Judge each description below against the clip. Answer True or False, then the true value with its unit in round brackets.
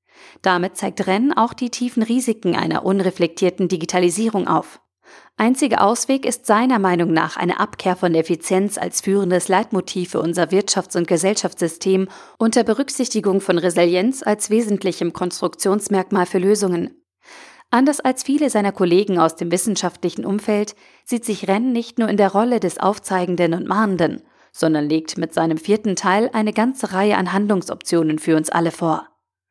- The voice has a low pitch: False (195 Hz)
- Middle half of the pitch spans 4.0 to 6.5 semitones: False (3.4 semitones)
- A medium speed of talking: True (150 wpm)